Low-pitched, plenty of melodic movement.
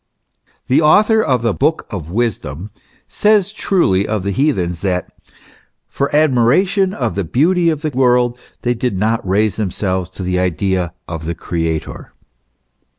Yes: low, 110 Hz; wide, 8.3 semitones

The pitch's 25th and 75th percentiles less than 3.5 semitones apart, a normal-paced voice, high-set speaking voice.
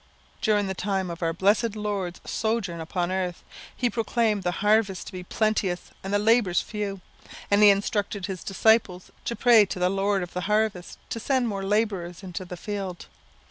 Yes: average, 2.9 semitones; average, 180 wpm; high, 200 Hz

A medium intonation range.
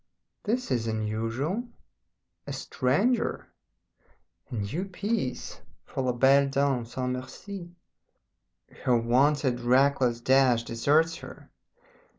Yes: average, 4.6 semitones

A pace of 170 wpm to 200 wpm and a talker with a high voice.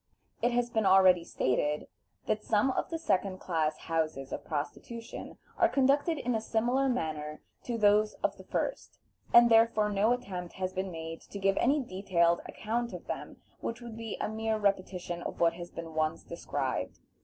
Yes: average, 180 wpm; high, 200 Hz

